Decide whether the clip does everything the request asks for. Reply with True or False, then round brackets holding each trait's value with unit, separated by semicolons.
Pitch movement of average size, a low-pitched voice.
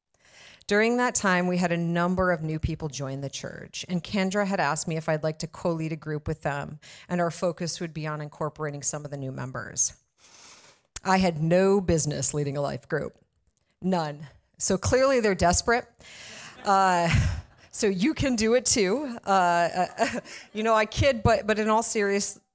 False (4.7 semitones; 175 Hz)